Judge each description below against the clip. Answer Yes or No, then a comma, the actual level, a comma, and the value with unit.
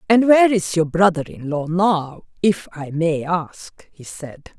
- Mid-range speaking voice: Yes, medium, 175 Hz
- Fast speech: No, average, 185 wpm